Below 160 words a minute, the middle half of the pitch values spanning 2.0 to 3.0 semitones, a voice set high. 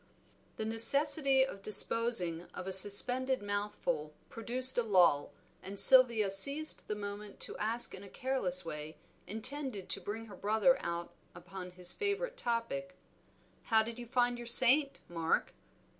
No: average, 145 wpm; average, 5.1 semitones; high, 220 Hz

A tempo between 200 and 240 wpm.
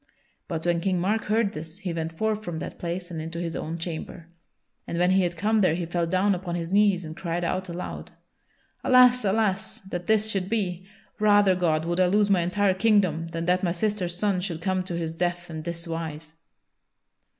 Yes: fast, 205 wpm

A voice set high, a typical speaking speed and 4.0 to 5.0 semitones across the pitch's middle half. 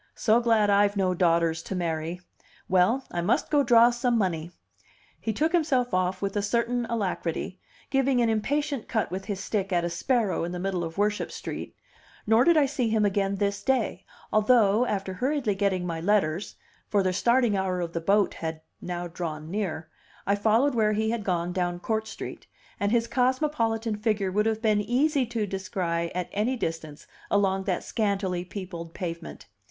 Yes: high, 205 Hz; average, 180 wpm; average, 4.4 semitones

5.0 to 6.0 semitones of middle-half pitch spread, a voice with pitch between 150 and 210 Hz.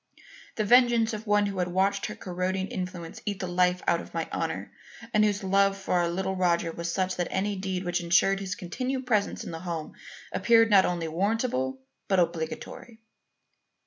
No: average, 2.7 semitones; high, 190 Hz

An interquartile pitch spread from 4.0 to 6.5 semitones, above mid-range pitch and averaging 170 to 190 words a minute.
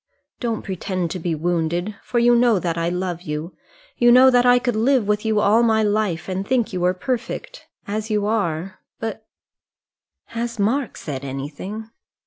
Yes: average, 4.9 semitones; high, 210 Hz; average, 180 wpm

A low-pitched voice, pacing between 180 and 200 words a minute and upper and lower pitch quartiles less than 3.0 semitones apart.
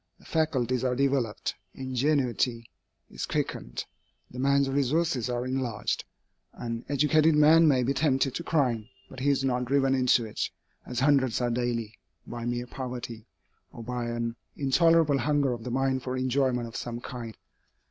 No: low, 130 Hz; average, 160 wpm; narrow, 2.5 semitones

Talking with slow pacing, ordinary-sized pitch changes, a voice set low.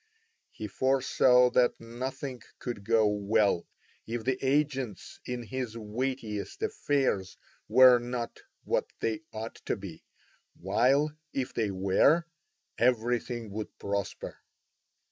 Yes: slow, 110 wpm; average, 3.4 semitones; low, 120 Hz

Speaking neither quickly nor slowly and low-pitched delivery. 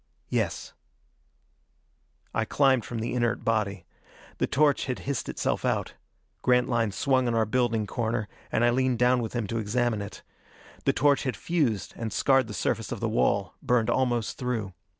Yes: average, 170 wpm; low, 120 Hz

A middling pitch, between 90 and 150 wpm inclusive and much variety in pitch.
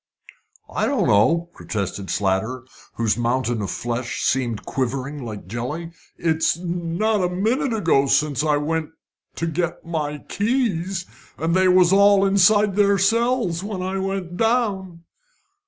Yes: medium, 170 Hz; average, 140 wpm; wide, 6.6 semitones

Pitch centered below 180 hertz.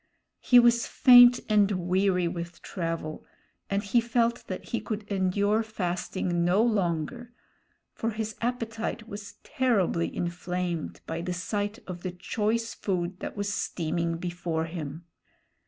No: high, 195 Hz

